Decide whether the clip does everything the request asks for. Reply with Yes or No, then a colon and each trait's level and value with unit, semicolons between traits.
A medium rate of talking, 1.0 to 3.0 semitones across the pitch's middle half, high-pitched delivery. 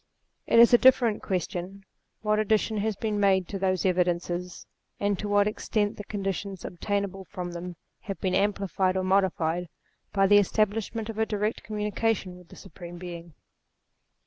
Yes: average, 165 wpm; narrow, 2.6 semitones; high, 195 Hz